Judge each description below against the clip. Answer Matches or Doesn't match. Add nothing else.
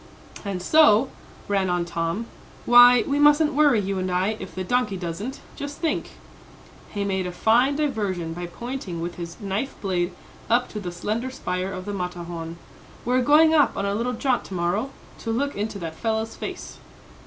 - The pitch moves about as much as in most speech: Doesn't match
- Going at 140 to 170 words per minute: Doesn't match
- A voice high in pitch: Matches